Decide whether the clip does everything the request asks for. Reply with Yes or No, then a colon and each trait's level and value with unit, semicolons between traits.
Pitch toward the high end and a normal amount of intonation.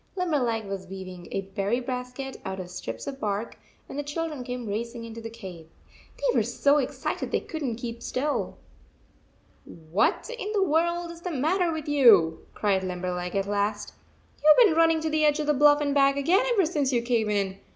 No: very high, 250 Hz; wide, 7.1 semitones